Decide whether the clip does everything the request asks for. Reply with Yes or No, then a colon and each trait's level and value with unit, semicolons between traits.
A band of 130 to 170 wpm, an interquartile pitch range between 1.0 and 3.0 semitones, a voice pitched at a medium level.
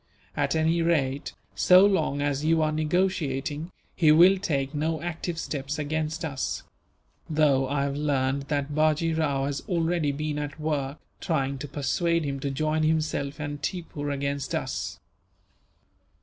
Yes: average, 150 wpm; narrow, 2.4 semitones; medium, 150 Hz